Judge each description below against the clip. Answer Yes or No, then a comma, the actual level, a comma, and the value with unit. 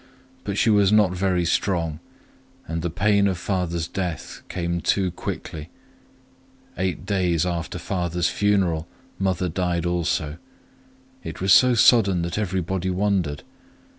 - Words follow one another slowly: Yes, slow, 130 wpm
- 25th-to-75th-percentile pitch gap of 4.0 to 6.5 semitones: No, narrow, 2.4 semitones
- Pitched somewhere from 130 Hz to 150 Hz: No, very low, 90 Hz